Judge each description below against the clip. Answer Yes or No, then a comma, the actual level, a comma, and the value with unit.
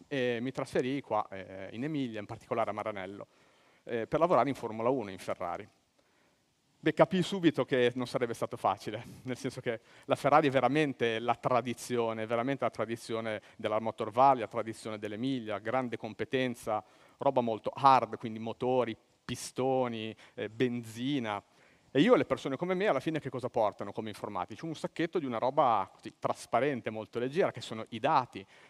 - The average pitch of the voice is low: Yes, low, 125 Hz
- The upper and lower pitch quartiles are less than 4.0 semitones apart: Yes, average, 3.3 semitones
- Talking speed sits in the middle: No, fast, 175 wpm